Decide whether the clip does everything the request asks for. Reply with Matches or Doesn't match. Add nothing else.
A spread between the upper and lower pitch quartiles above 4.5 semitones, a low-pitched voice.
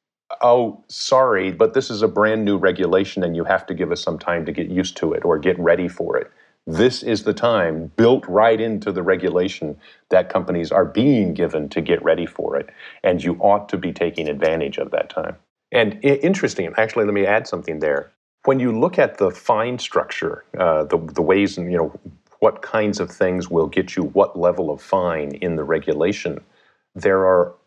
Matches